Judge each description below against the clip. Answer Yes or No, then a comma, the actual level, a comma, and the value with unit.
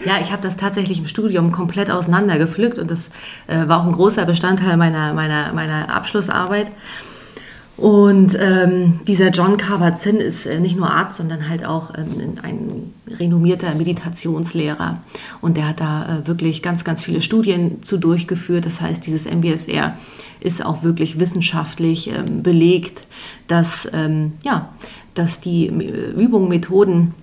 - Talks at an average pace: Yes, average, 150 wpm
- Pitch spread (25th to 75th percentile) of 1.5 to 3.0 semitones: Yes, average, 2.7 semitones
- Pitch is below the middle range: No, medium, 175 Hz